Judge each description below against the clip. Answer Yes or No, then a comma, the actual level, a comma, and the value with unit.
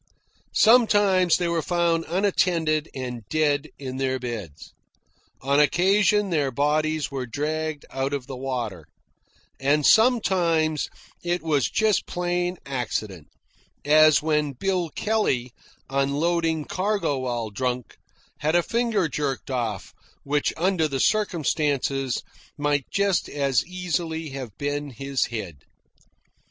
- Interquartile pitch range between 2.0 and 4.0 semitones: No, average, 4.6 semitones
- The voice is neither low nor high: Yes, medium, 150 Hz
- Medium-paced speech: No, slow, 120 wpm